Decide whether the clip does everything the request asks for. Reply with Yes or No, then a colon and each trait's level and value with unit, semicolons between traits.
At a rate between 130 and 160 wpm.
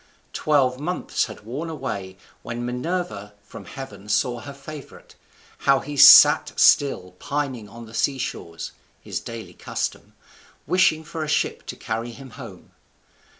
Yes: average, 140 wpm